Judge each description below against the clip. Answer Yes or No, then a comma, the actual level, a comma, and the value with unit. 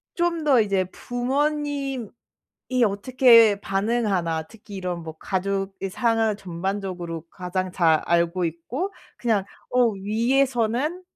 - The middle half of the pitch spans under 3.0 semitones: No, average, 5.2 semitones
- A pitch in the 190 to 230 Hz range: Yes, high, 205 Hz